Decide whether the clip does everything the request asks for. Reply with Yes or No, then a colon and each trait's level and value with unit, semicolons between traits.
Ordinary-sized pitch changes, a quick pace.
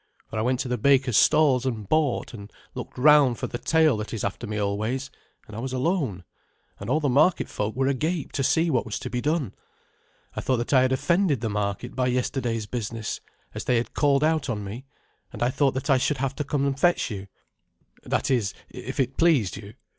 Yes: average, 4.0 semitones; fast, 220 wpm